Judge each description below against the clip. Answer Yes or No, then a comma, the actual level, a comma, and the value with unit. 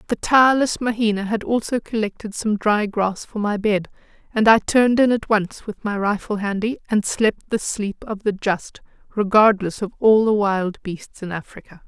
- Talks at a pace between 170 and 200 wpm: Yes, average, 185 wpm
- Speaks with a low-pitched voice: No, high, 210 Hz